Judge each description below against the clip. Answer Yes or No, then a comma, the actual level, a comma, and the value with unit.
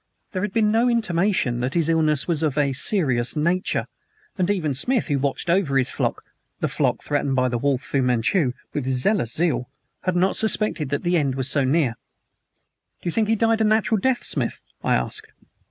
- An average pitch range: No, wide, 6.8 semitones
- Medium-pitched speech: Yes, medium, 155 Hz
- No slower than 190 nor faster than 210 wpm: Yes, average, 200 wpm